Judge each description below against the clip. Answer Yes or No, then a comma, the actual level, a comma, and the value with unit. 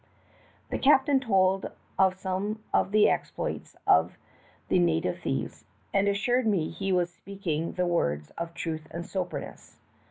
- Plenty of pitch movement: No, average, 3.1 semitones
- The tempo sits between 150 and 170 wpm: No, average, 140 wpm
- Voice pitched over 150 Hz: Yes, medium, 185 Hz